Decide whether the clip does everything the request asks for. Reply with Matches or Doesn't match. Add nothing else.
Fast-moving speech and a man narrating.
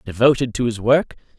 Doesn't match